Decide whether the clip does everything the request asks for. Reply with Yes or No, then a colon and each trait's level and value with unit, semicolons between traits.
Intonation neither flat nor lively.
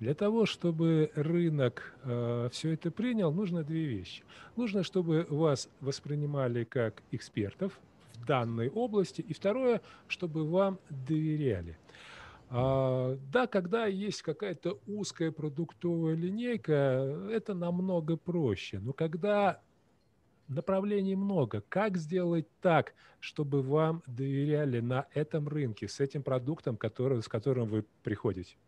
No: wide, 5.7 semitones